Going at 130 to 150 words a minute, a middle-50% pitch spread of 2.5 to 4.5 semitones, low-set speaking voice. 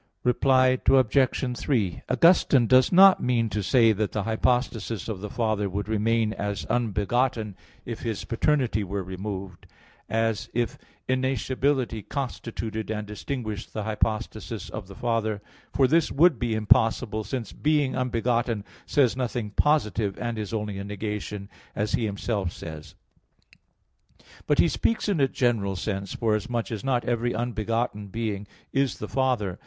Yes: average, 145 wpm; average, 3.4 semitones; low, 115 Hz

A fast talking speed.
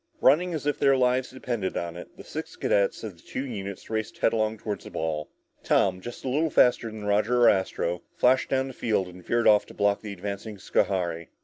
Yes: fast, 215 wpm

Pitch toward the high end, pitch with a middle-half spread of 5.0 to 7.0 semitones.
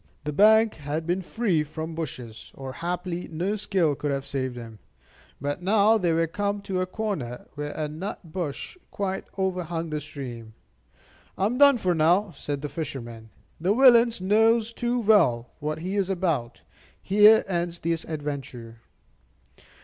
No: medium, 170 Hz; wide, 5.6 semitones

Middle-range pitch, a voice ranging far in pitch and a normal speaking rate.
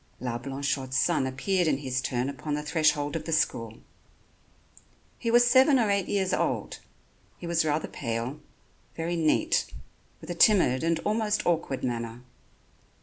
Yes: medium, 155 Hz; wide, 6.1 semitones; average, 150 wpm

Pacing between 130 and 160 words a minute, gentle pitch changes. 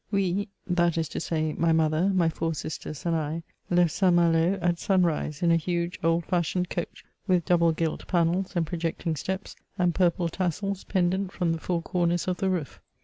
No: average, 190 wpm; narrow, 1.8 semitones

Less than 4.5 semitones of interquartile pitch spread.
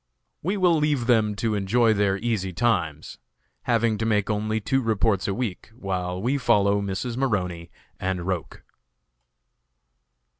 Yes: average, 3.7 semitones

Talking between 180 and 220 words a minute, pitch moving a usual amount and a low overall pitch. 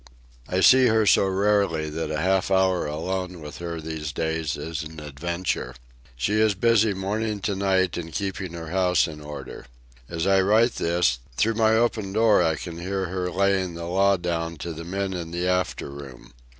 Yes: average, 190 wpm; average, 3.2 semitones; very low, 90 Hz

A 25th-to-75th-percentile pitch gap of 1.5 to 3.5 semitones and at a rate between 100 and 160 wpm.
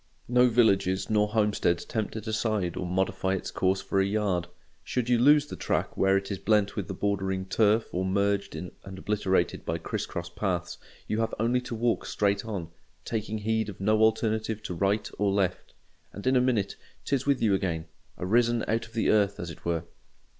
No: average, 2.7 semitones; average, 195 wpm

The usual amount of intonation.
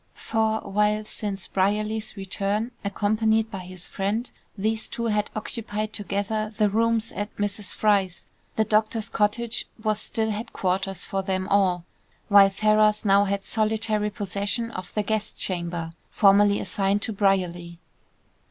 No: narrow, 1.8 semitones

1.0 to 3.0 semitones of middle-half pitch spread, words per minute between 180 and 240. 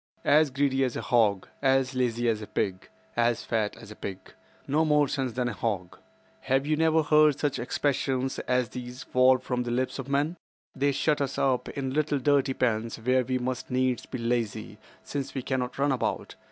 Yes: narrow, 2.6 semitones; average, 195 wpm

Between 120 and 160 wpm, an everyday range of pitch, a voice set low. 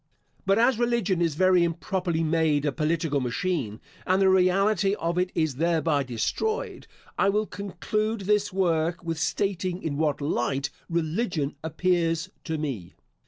No: average, 145 wpm; average, 3.7 semitones; medium, 170 Hz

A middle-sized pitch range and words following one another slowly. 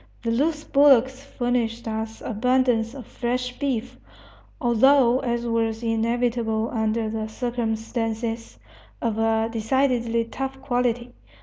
No: narrow, 2.0 semitones; slow, 110 wpm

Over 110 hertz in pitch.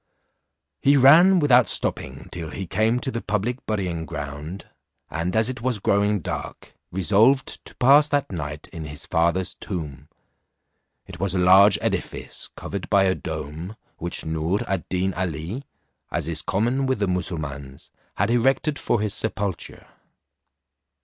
No: very low, 95 Hz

